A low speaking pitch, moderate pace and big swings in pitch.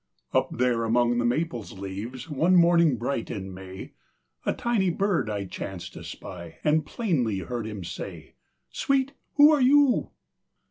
Yes: low, 125 Hz; average, 150 wpm; wide, 8.8 semitones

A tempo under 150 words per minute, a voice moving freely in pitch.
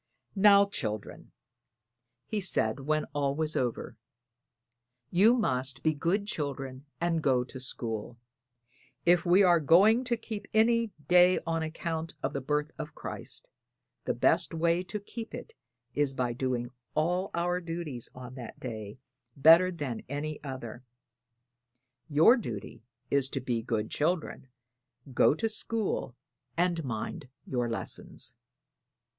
Yes: slow, 135 wpm; wide, 5.7 semitones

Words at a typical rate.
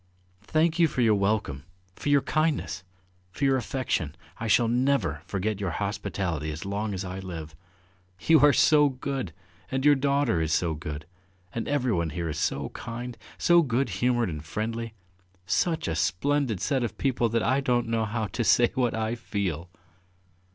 Yes: average, 170 wpm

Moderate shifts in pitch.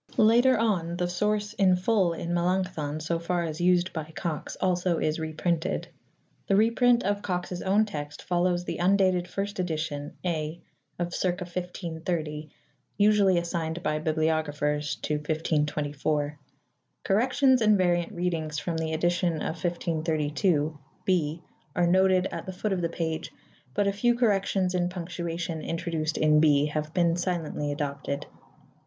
Yes: average, 3.0 semitones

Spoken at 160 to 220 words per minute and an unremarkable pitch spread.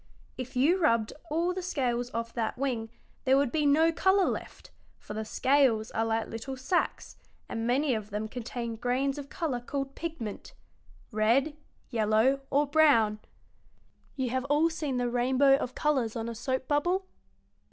Yes: average, 165 wpm; average, 4.0 semitones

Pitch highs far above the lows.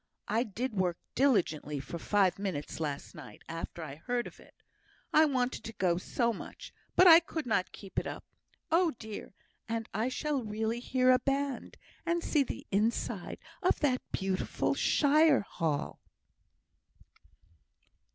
Yes: wide, 6.7 semitones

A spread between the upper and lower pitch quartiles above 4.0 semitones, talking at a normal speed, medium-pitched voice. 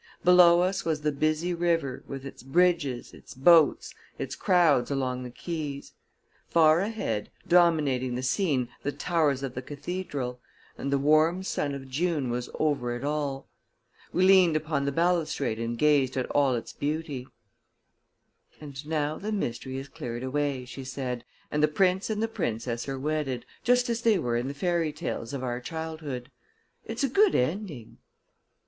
Yes: average, 4.7 semitones; average, 165 wpm; medium, 145 Hz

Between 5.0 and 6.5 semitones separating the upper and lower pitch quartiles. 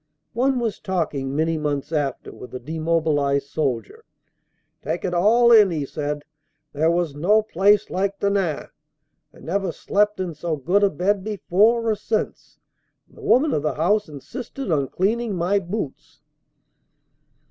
Yes: wide, 5.5 semitones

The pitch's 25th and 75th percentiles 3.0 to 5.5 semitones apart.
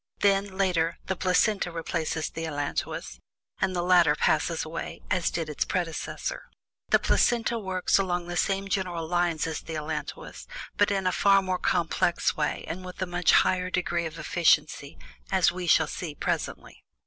No: narrow, 2.4 semitones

